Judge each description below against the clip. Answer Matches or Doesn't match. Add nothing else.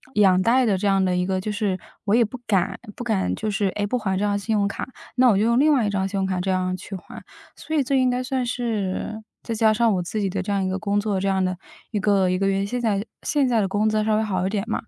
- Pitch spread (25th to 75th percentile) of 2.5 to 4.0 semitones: Matches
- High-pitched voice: Matches